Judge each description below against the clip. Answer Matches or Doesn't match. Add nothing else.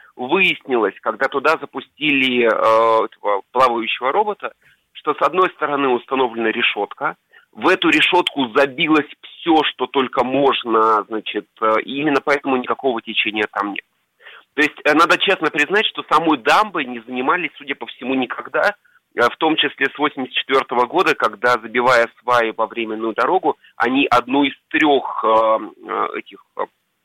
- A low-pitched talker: Matches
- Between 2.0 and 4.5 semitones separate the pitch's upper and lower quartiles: Matches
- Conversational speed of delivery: Matches